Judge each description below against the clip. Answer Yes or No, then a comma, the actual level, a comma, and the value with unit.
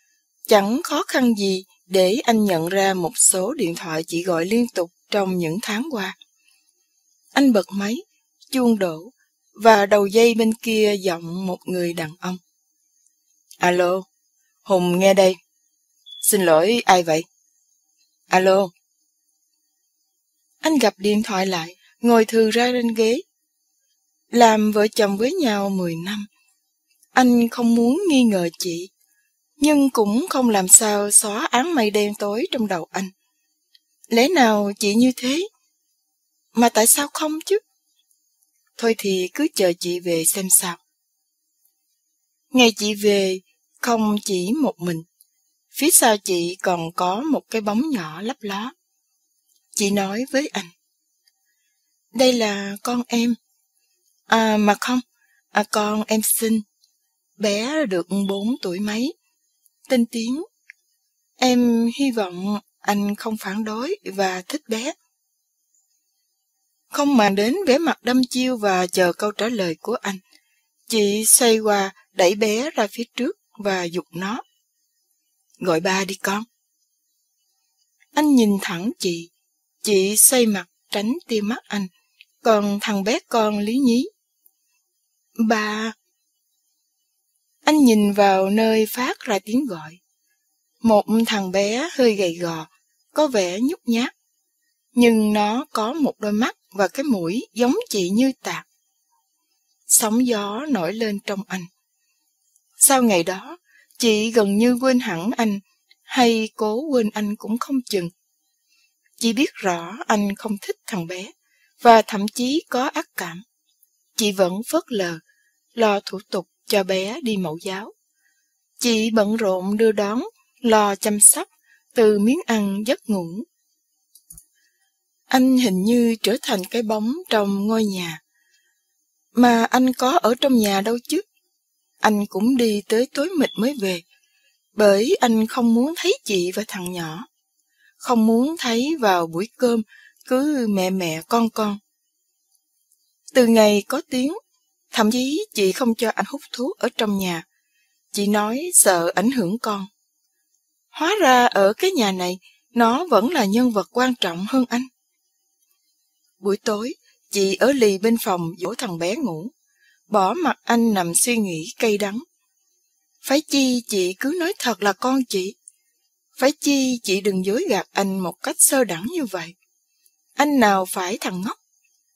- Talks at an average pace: No, slow, 145 wpm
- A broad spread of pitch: Yes, wide, 6.6 semitones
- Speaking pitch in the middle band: No, high, 225 Hz